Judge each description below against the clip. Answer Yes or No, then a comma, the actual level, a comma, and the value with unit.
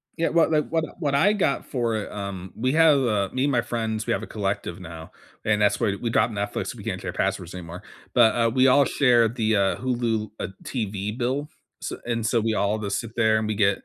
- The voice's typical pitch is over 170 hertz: No, low, 115 Hz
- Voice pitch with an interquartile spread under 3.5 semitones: No, average, 3.8 semitones